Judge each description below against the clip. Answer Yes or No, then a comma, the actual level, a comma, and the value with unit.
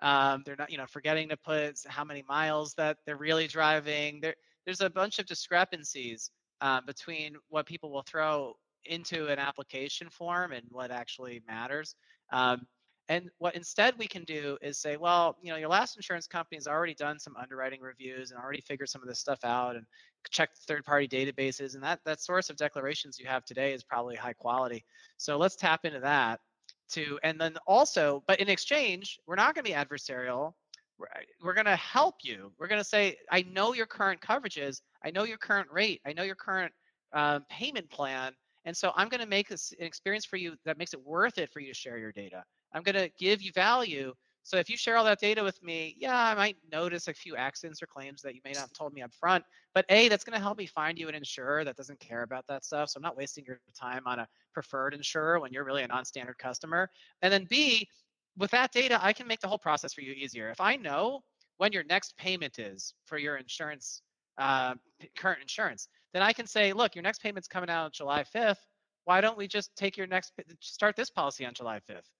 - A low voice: No, medium, 155 Hz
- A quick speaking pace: Yes, fast, 225 wpm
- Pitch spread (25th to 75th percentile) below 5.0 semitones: No, wide, 5.5 semitones